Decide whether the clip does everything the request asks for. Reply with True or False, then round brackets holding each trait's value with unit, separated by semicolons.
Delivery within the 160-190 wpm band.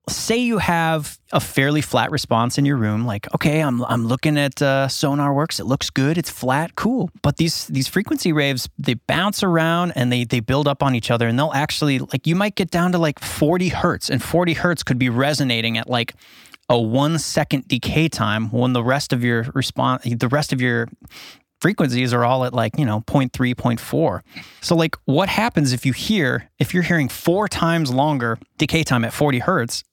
False (205 wpm)